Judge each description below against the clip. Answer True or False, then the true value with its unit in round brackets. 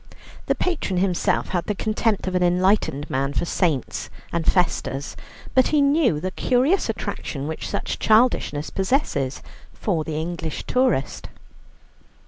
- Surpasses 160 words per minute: False (135 wpm)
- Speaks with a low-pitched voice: False (180 Hz)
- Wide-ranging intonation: True (6.3 semitones)